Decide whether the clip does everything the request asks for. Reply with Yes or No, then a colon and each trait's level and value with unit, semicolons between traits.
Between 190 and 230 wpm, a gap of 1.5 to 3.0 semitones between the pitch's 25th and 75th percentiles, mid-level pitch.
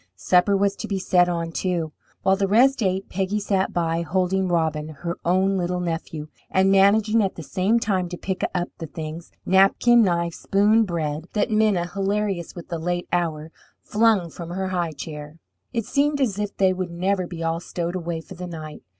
Yes: average, 195 wpm; narrow, 2.6 semitones; medium, 180 Hz